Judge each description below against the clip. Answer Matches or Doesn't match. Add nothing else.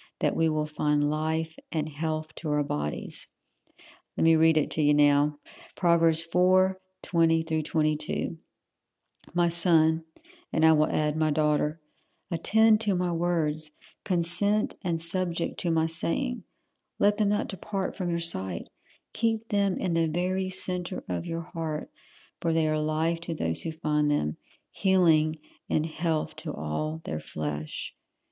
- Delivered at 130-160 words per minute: Matches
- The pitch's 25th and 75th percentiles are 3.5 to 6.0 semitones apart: Doesn't match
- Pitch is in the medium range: Matches